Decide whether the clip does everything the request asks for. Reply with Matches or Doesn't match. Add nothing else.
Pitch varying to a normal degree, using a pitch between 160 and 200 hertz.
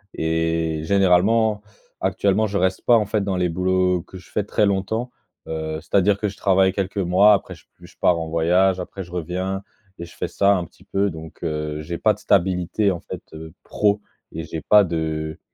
Doesn't match